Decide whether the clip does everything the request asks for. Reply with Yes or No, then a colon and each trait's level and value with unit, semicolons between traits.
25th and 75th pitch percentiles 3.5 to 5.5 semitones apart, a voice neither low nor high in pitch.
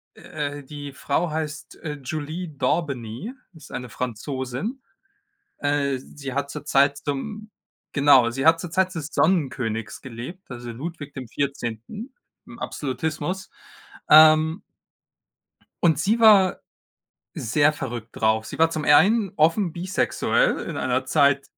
Yes: average, 4.1 semitones; medium, 145 Hz